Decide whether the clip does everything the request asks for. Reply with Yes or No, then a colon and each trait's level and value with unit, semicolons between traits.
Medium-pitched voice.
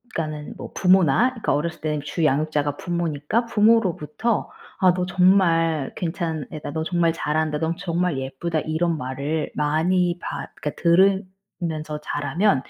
Yes: medium, 165 Hz